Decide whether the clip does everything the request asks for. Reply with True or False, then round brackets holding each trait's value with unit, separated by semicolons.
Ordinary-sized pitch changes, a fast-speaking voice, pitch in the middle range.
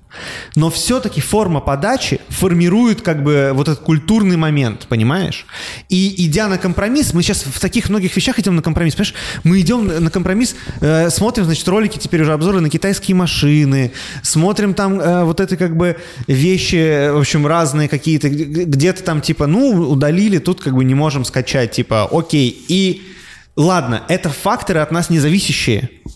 True (4.2 semitones; 165 wpm; 165 Hz)